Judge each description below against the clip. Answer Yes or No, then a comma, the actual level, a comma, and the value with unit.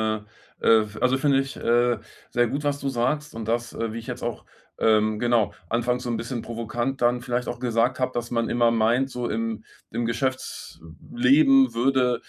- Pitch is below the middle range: Yes, low, 120 Hz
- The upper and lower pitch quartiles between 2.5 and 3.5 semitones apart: No, narrow, 2.1 semitones